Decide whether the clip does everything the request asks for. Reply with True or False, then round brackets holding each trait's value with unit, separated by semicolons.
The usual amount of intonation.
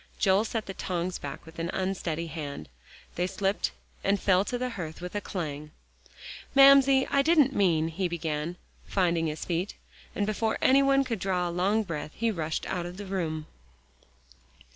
True (4.5 semitones)